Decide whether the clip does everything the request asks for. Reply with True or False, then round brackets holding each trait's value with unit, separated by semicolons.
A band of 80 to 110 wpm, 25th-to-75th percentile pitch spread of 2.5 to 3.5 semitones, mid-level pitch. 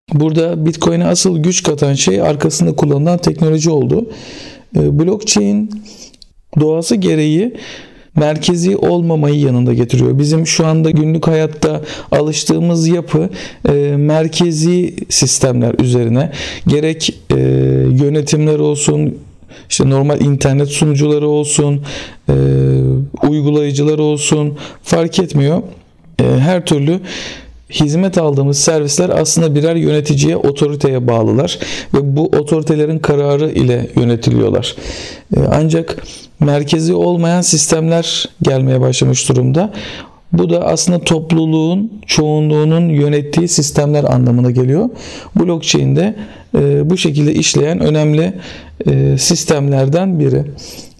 True (100 wpm; 2.9 semitones; 150 Hz)